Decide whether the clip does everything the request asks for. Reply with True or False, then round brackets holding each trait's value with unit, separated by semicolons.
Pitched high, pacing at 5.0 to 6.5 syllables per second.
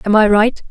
True (215 Hz; 5.4 syllables/s)